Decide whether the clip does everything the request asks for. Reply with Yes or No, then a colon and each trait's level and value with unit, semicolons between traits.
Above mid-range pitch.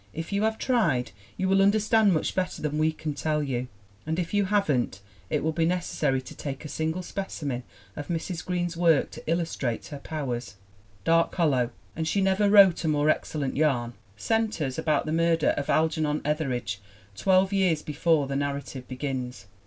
No: medium, 155 Hz